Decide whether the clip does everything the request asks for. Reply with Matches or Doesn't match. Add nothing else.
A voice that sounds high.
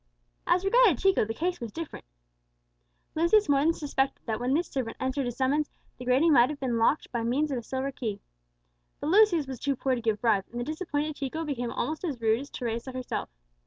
Matches